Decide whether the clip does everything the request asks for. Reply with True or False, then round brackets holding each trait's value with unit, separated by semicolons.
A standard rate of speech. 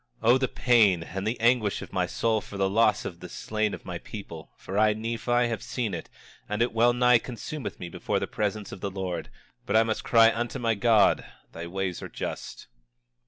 False (215 wpm)